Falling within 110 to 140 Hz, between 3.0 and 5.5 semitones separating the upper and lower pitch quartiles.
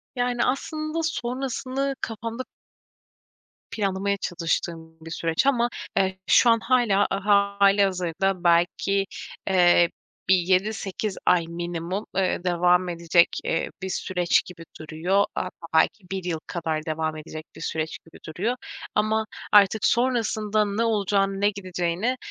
No: high, 195 Hz; average, 4.0 semitones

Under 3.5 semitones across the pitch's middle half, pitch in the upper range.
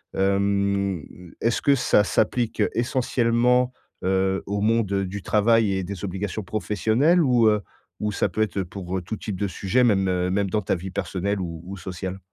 No: average, 2.9 semitones; low, 100 Hz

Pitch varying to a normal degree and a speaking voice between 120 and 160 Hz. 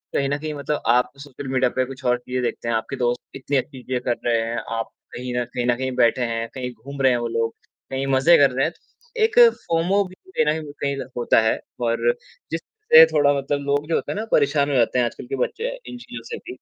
Yes: average, 3.5 semitones; low, 135 Hz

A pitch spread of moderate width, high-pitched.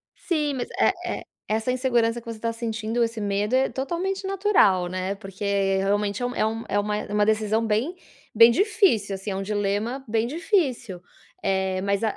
Yes: average, 3.8 semitones; high, 220 Hz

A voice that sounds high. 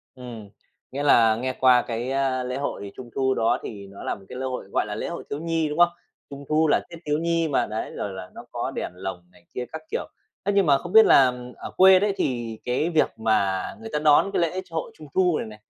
No: low, 135 Hz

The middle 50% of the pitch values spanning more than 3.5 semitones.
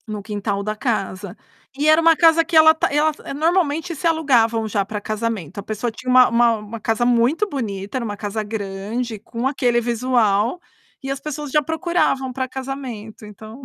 Yes: average, 5.2 semitones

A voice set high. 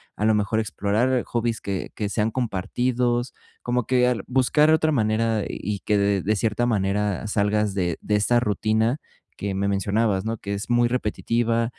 No: low, 110 Hz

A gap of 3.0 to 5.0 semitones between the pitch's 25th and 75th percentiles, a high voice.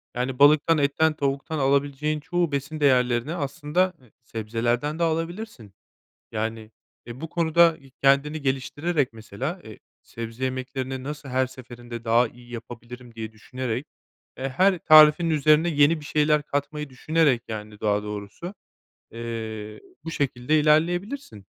No: average, 4.5 semitones; low, 135 Hz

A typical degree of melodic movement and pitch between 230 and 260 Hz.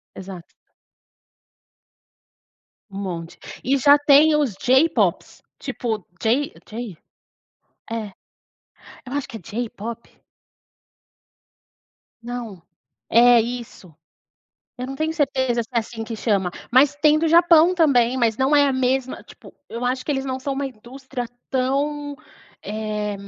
Yes: average, 4.0 semitones; very high, 250 Hz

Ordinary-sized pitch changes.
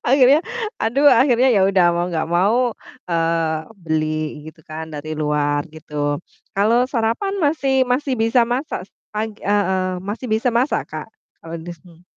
No: wide, 7.5 semitones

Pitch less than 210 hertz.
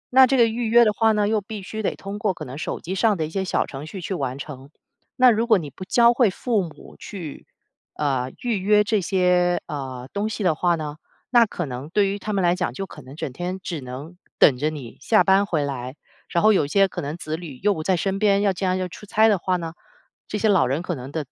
Yes: medium, 185 Hz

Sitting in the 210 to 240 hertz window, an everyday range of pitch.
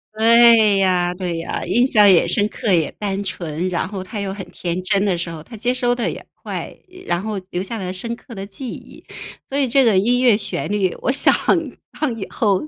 No: high, 200 Hz; average, 4.1 semitones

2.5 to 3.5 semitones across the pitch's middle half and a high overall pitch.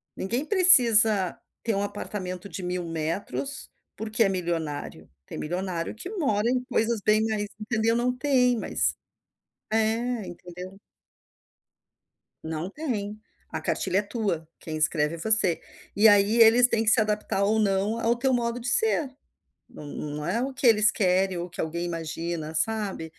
No: average, 4.6 semitones; high, 210 Hz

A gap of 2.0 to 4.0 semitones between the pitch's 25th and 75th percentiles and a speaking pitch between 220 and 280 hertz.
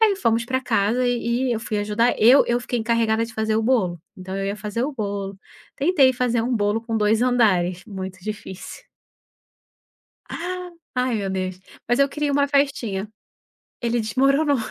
Yes: average, 3.6 semitones; high, 230 Hz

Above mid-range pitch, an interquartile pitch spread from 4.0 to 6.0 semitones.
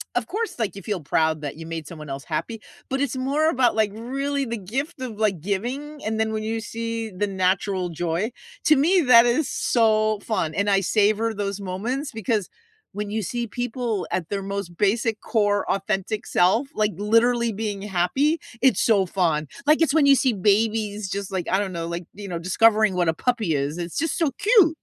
Yes: high, 215 Hz; average, 4.3 semitones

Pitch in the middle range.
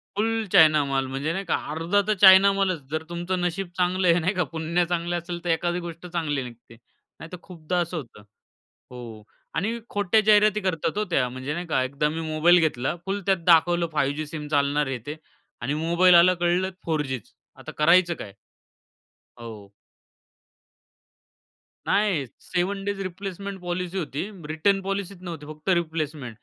Yes: medium, 170 Hz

